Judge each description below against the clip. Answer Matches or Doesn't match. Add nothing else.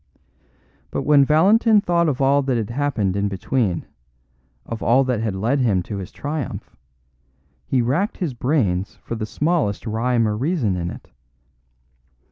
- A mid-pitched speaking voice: Doesn't match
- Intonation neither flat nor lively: Doesn't match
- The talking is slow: Doesn't match